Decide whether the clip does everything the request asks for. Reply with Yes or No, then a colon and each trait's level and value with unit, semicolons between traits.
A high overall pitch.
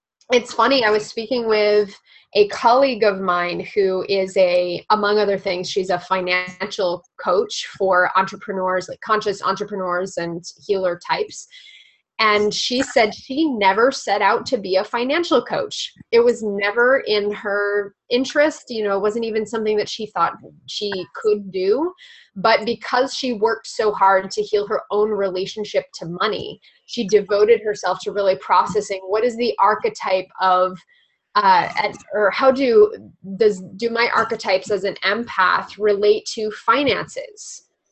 Yes: high, 210 Hz